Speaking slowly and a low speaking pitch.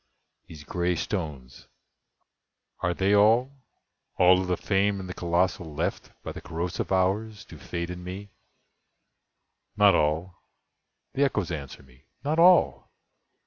Yes: slow, 120 wpm; very low, 90 Hz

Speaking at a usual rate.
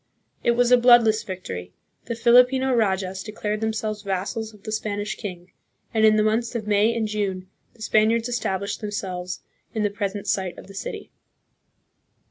Yes: average, 165 wpm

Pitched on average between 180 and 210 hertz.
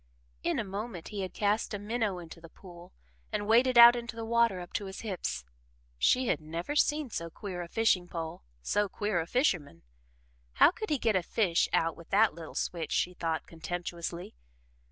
Yes: high, 190 Hz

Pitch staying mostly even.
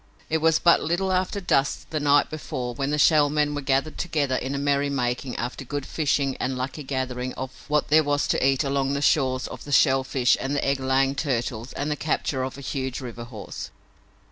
Yes: narrow, 2.1 semitones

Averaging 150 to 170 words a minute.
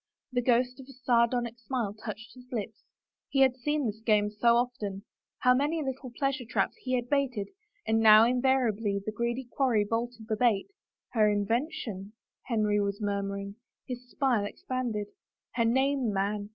No: average, 185 wpm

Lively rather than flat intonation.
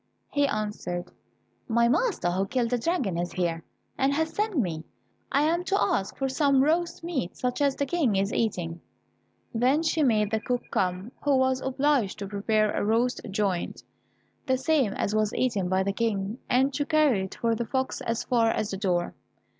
Yes: wide, 5.9 semitones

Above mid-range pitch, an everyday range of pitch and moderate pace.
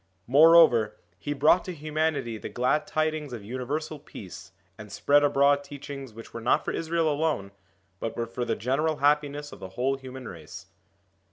No: medium, 140 Hz; average, 4.6 semitones; average, 175 wpm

